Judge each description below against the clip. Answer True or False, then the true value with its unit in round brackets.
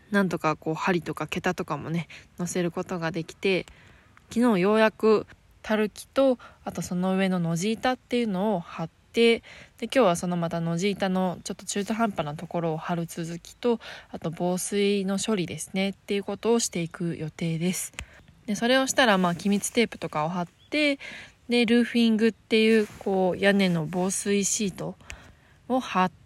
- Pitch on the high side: True (195 Hz)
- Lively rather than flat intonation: False (4.4 semitones)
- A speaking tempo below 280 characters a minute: False (355 characters per minute)